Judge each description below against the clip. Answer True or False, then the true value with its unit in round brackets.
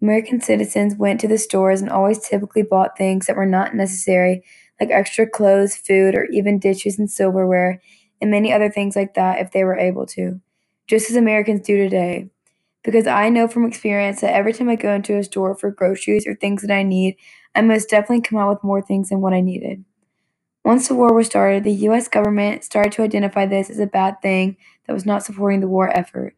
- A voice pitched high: True (200 Hz)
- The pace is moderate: False (215 wpm)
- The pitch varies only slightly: True (1.9 semitones)